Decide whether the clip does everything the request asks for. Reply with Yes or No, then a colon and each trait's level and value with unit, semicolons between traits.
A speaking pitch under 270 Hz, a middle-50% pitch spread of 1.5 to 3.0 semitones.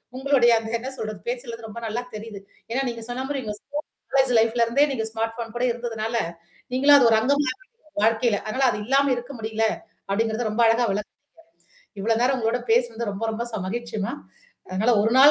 Yes: high, 235 Hz; narrow, 2.4 semitones